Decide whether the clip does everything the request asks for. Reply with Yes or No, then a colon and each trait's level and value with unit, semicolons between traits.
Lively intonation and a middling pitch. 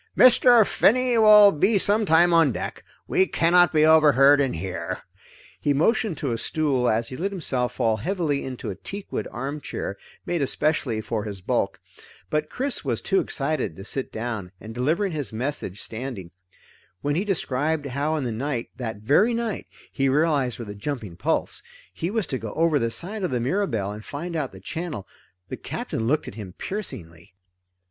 Yes: wide, 7.0 semitones; medium, 145 Hz